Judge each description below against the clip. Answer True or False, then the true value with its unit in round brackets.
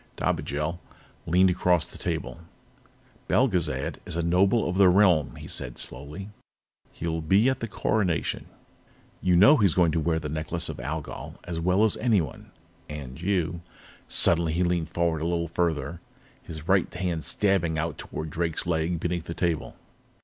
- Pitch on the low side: True (85 Hz)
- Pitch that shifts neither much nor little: False (2.3 semitones)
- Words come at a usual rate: True (165 wpm)